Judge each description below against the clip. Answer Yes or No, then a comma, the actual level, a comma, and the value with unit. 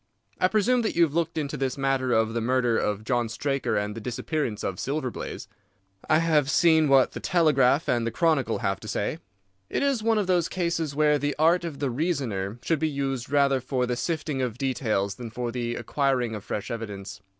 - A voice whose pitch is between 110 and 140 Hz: Yes, low, 135 Hz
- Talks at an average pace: No, fast, 210 wpm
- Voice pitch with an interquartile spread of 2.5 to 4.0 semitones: No, average, 5.0 semitones